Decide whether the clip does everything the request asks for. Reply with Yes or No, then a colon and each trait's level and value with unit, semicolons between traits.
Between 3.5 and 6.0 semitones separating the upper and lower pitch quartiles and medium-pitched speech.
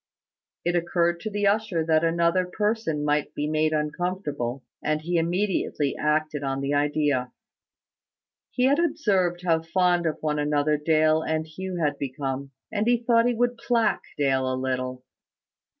Yes: average, 4.2 semitones; medium, 160 Hz